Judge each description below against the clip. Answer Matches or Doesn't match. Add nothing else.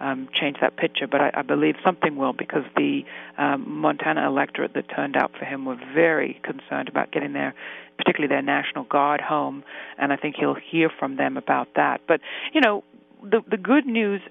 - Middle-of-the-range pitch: Matches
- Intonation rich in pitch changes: Matches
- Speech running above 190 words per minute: Matches